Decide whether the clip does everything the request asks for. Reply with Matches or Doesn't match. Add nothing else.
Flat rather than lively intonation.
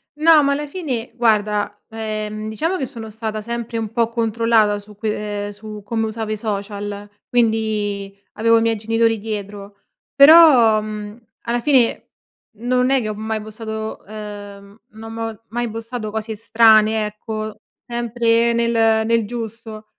Matches